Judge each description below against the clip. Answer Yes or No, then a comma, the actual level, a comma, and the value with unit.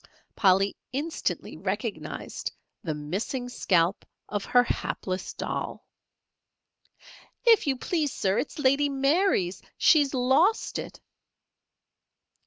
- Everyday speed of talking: No, slow, 95 wpm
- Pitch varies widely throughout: Yes, wide, 7.2 semitones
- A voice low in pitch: No, very high, 255 Hz